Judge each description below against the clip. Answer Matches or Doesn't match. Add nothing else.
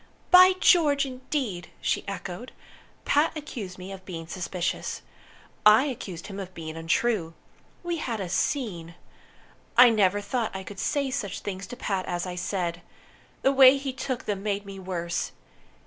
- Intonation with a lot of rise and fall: Matches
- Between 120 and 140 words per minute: Doesn't match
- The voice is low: Doesn't match